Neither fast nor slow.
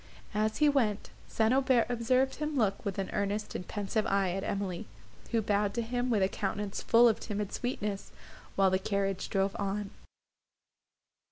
Yes: average, 170 wpm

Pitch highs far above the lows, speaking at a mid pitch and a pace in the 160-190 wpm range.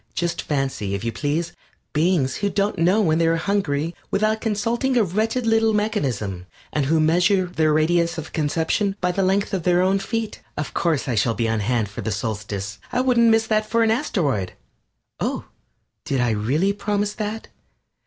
Yes: wide, 7.4 semitones; medium, 175 Hz; average, 185 wpm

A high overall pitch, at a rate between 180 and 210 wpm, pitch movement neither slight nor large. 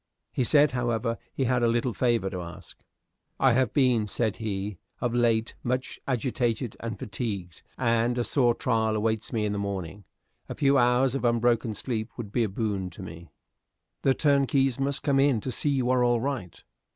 No: low, 120 Hz; average, 190 wpm; average, 3.1 semitones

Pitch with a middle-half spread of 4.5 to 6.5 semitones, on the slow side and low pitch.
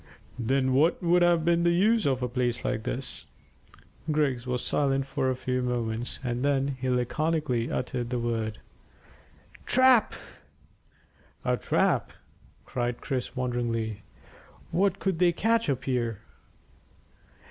Yes: average, 5.1 semitones; slow, 130 wpm; low, 130 Hz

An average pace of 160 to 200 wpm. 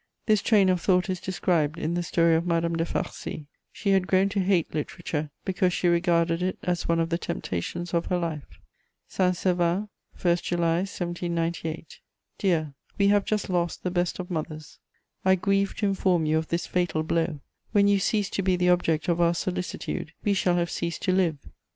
Yes: average, 195 wpm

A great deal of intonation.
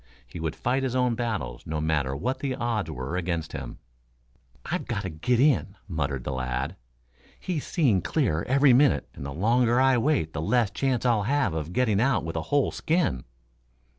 Yes: wide, 8.4 semitones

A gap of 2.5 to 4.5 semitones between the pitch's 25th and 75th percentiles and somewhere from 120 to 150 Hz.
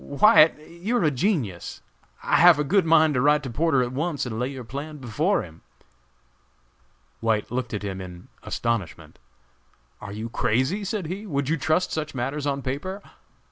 No: wide, 5.4 semitones; medium, 140 Hz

